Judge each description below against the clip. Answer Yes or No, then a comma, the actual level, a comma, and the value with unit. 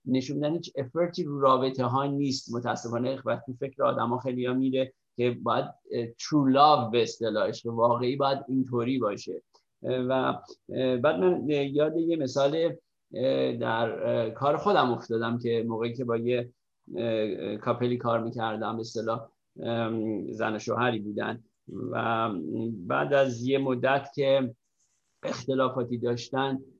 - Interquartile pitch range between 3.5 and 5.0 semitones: No, average, 2.9 semitones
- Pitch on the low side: Yes, low, 125 Hz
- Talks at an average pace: Yes, average, 125 wpm